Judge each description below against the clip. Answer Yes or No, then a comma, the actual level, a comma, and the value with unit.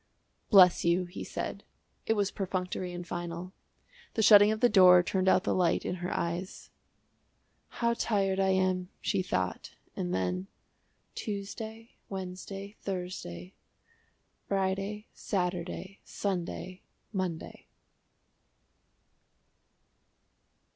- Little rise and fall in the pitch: Yes, narrow, 2.0 semitones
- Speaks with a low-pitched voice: No, medium, 185 Hz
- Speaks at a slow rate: Yes, slow, 105 wpm